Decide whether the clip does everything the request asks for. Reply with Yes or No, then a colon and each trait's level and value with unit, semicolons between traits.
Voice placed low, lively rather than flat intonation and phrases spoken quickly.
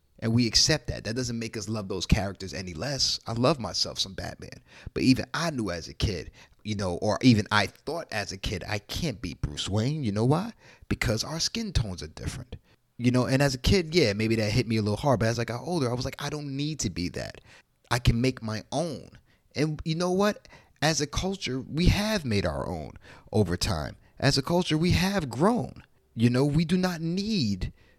Yes: low, 120 Hz; wide, 6.4 semitones; fast, 230 wpm